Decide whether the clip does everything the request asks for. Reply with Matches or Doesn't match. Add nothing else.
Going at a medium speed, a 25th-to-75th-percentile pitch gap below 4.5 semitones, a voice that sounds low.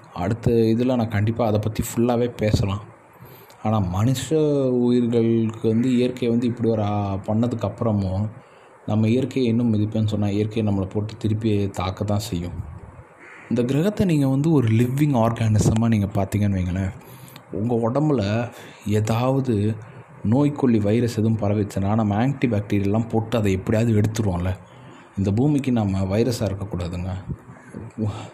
Matches